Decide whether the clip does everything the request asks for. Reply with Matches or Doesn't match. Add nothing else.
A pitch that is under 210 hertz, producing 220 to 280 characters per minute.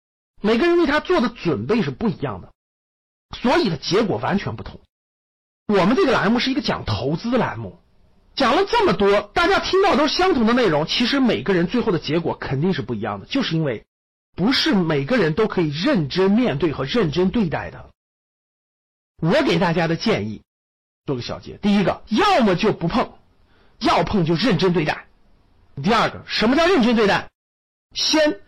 Matches